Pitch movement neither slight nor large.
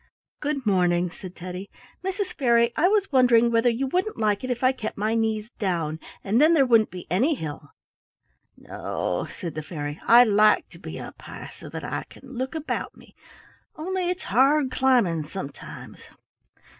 No: wide, 6.4 semitones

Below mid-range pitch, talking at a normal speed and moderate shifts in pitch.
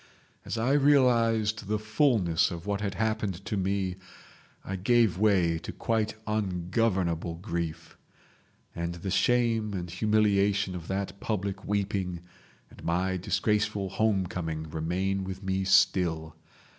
No: very low, 95 Hz; slow, 125 wpm; average, 3.2 semitones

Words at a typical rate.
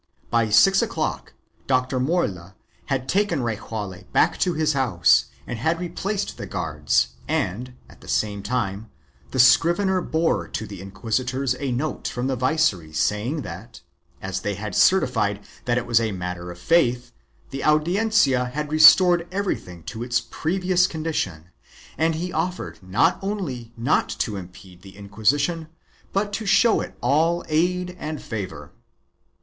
Yes: average, 150 wpm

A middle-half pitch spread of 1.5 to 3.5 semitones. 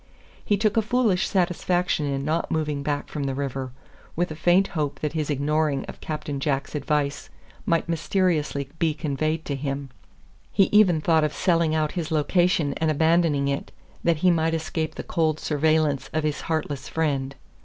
Yes: average, 2.7 semitones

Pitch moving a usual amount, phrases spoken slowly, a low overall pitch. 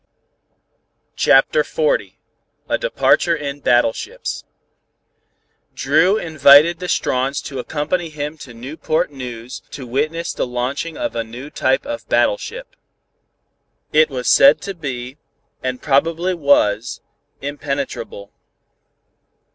No: average, 4.7 semitones; slow, 105 wpm; medium, 145 Hz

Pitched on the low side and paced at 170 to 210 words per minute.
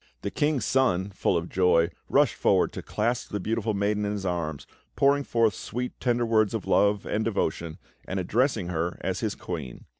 Yes: low, 105 Hz; average, 185 wpm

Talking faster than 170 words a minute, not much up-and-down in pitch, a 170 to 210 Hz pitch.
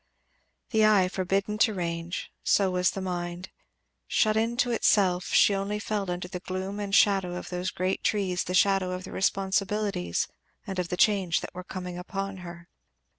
Yes: average, 180 wpm; narrow, 2.0 semitones; high, 190 Hz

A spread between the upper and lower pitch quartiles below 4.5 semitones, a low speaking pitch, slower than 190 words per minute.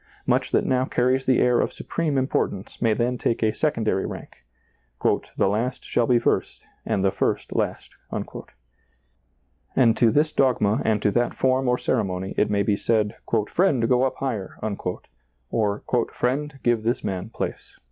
Yes: average, 3.7 semitones; low, 120 Hz; average, 175 wpm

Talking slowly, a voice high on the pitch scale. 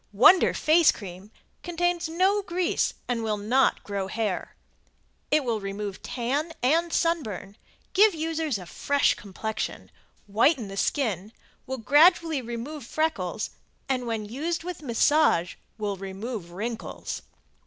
Yes: slow, 130 wpm; very high, 250 Hz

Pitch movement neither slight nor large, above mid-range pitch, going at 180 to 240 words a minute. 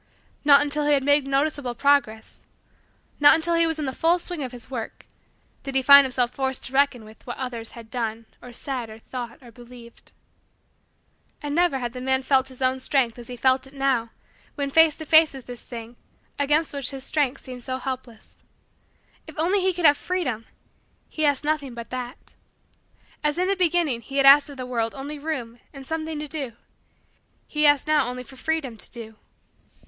Yes: average, 3.3 semitones; very high, 270 Hz; average, 200 wpm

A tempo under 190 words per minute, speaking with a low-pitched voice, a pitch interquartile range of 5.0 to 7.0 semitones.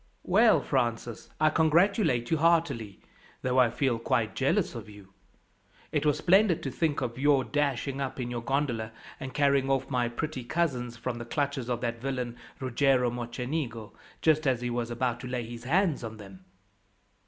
No: average, 175 wpm; low, 130 Hz; average, 3.7 semitones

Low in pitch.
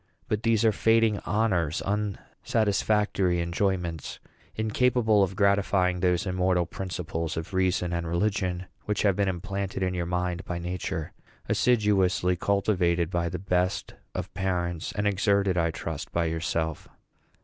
Yes: very low, 95 Hz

